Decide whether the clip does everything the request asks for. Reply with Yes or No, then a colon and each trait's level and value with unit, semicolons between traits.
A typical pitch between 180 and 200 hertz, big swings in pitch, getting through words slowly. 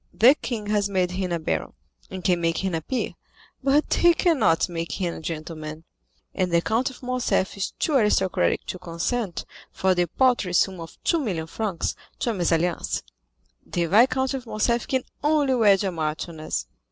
No: high, 190 Hz; wide, 6.4 semitones; average, 175 wpm